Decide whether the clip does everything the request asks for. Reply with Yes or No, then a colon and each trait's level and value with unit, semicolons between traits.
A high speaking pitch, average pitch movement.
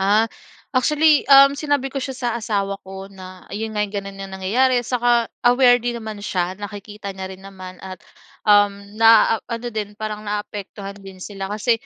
Yes: high, 210 Hz; average, 3.6 semitones